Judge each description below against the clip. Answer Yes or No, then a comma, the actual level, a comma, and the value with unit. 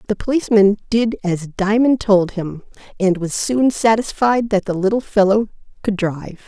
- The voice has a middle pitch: No, high, 205 Hz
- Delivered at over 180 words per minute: No, average, 155 wpm